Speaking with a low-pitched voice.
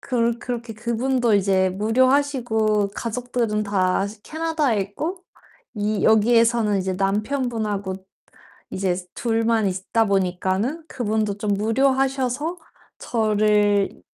No: high, 220 Hz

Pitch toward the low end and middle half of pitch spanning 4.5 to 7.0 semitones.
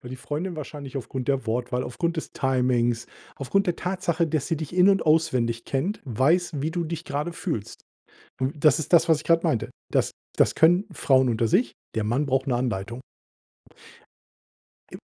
No: medium, 145 Hz; average, 5.0 semitones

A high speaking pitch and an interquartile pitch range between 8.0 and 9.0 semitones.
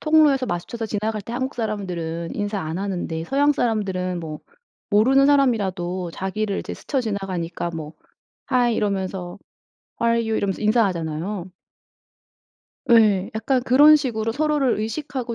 No: high, 215 Hz; average, 5.1 semitones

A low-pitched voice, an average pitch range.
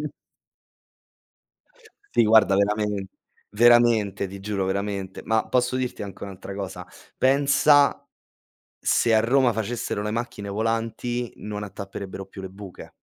Yes: low, 105 Hz; average, 3.3 semitones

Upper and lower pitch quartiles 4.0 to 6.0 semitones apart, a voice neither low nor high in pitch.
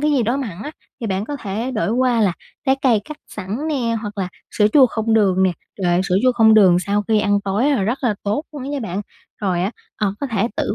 No: average, 4.4 semitones; high, 220 Hz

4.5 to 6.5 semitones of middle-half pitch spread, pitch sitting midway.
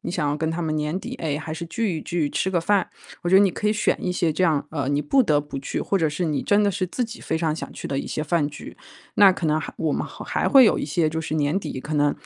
No: average, 3.9 semitones; medium, 160 Hz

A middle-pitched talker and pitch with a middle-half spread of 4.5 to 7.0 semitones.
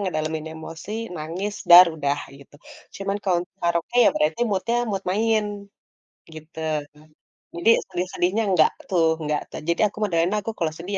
No: medium, 175 Hz; average, 3.7 semitones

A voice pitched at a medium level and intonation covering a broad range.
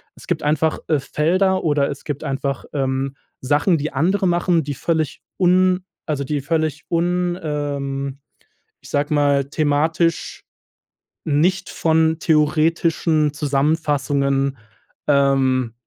No: medium, 150 Hz; average, 2.9 semitones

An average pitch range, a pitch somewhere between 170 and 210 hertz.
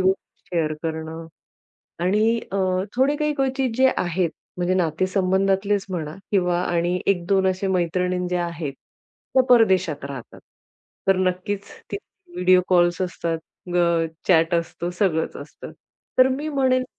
Yes: average, 3.0 semitones; medium, 185 Hz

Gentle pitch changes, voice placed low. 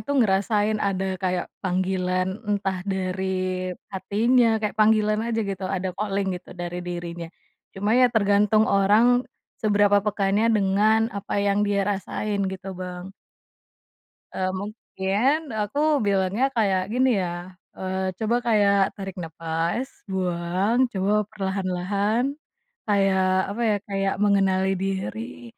No: narrow, 2.3 semitones; high, 195 Hz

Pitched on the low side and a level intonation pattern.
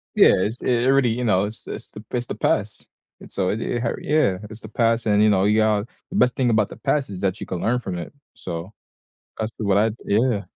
No: low, 110 Hz; average, 3.1 semitones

